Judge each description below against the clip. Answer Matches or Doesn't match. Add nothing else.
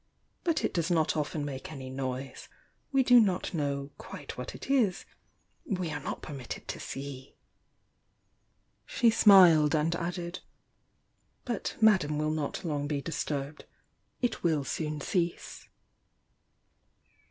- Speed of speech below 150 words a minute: Matches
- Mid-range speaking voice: Matches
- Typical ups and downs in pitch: Matches